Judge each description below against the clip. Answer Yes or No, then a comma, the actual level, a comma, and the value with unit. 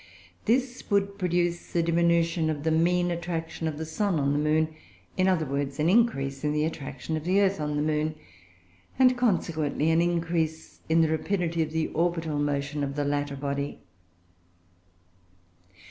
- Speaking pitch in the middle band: Yes, medium, 160 Hz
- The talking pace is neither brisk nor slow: Yes, average, 170 wpm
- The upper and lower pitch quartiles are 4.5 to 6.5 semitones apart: No, average, 2.8 semitones